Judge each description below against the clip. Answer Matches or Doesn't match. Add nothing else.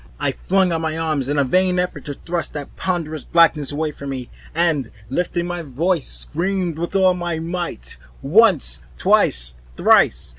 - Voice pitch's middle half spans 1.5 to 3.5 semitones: Doesn't match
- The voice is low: Doesn't match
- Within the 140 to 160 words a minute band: Doesn't match